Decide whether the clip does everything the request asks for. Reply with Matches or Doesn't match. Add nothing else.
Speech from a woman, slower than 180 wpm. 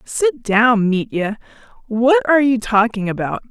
Matches